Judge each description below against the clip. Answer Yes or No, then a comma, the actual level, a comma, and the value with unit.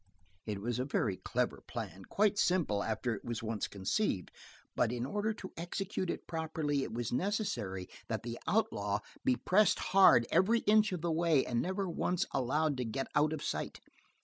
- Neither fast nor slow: Yes, average, 180 wpm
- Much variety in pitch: Yes, wide, 8.3 semitones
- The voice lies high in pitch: No, medium, 145 Hz